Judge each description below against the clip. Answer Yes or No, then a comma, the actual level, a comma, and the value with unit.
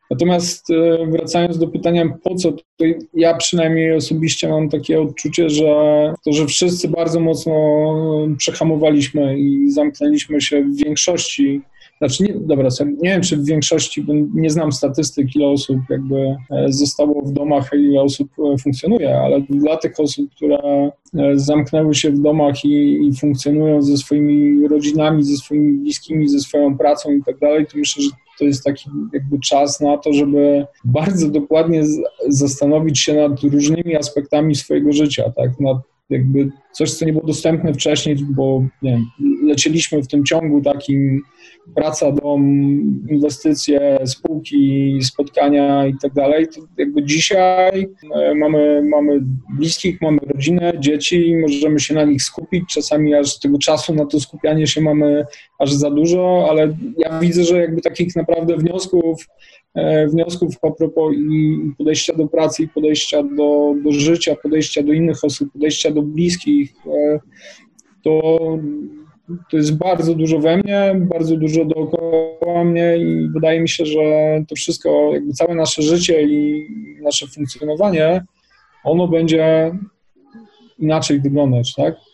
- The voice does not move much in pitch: Yes, narrow, 2.2 semitones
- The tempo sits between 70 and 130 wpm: No, average, 145 wpm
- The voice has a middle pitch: Yes, medium, 150 Hz